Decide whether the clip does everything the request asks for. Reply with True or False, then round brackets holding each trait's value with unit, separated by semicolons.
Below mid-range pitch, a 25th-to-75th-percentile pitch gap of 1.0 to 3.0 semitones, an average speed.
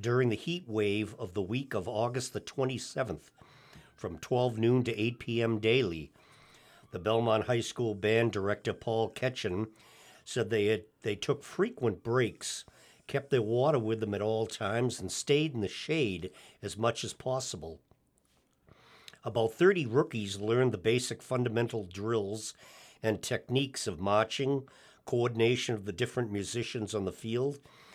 True (115 Hz; 2.6 semitones; 150 wpm)